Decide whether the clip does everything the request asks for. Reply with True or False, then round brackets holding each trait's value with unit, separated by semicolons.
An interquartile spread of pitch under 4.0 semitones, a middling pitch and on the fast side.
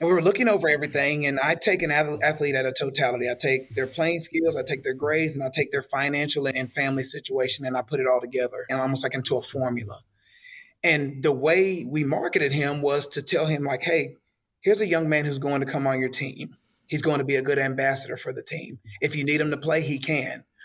True (2.9 semitones; 145 Hz; 245 wpm)